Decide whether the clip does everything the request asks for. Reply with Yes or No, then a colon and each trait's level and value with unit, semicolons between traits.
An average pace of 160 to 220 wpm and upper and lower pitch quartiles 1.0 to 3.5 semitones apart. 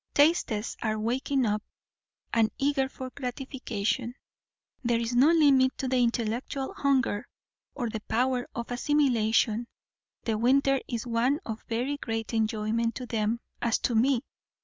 No: average, 140 wpm; average, 2.9 semitones